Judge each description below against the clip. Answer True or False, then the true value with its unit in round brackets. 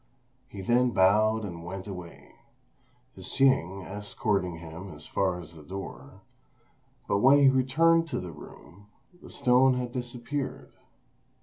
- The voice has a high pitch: False (100 Hz)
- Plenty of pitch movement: True (6.0 semitones)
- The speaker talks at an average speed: False (130 wpm)